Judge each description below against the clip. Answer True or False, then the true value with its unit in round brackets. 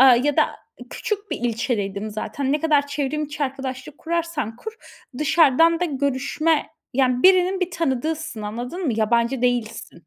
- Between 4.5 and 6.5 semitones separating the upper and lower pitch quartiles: True (4.8 semitones)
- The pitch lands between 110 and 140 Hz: False (280 Hz)